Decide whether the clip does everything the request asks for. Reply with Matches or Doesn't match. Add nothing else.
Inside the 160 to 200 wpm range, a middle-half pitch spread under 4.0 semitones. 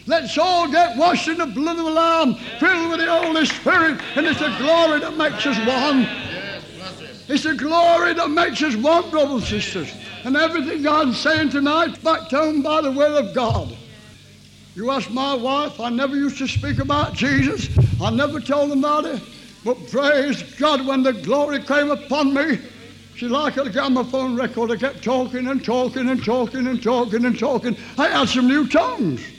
Matches